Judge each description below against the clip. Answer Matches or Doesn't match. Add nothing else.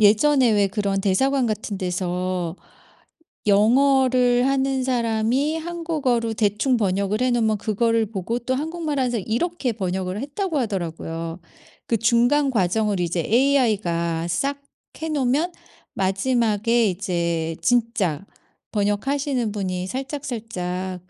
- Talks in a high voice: Matches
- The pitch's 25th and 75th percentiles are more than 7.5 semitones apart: Doesn't match